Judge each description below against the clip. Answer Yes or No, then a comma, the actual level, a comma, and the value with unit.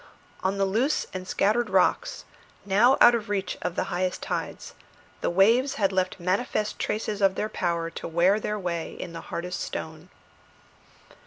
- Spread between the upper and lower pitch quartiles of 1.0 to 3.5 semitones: Yes, average, 2.9 semitones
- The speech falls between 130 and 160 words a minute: No, average, 170 wpm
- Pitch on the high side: Yes, high, 195 Hz